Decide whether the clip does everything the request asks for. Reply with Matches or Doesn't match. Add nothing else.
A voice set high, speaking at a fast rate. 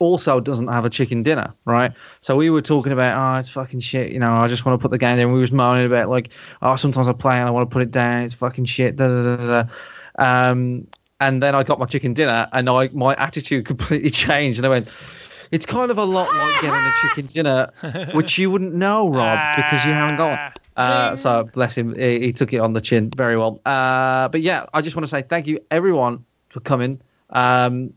Doesn't match